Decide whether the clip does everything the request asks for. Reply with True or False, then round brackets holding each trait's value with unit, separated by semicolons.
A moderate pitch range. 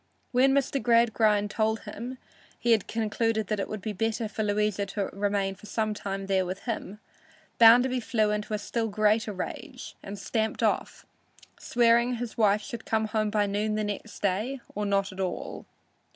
False (2.0 semitones)